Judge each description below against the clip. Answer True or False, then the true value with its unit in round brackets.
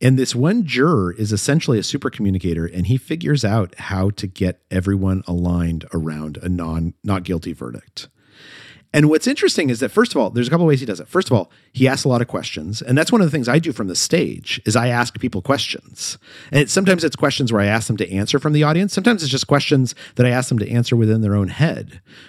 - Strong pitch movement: True (7.1 semitones)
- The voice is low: True (120 Hz)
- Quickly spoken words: True (250 wpm)